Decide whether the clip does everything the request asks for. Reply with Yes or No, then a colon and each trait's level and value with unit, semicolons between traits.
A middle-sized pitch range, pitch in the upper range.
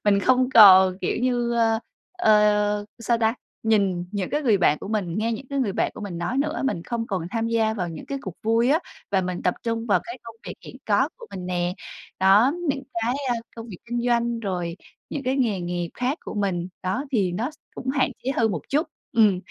Yes: average, 4.3 semitones; high, 220 Hz